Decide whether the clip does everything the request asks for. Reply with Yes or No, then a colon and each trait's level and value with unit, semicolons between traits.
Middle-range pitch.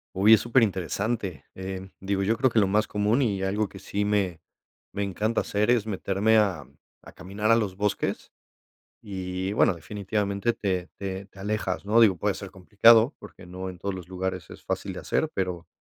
No: low, 100 Hz